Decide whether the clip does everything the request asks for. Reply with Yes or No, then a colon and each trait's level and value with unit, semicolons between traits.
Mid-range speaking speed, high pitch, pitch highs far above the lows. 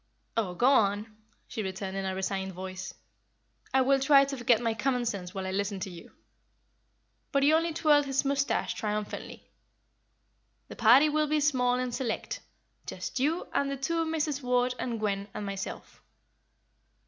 Yes: average, 165 wpm; high, 245 Hz; wide, 5.8 semitones